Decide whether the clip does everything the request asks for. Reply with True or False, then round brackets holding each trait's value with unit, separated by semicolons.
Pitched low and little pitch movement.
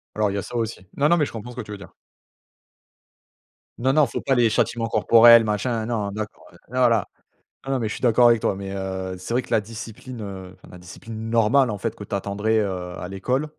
False (110 Hz; 3.1 semitones)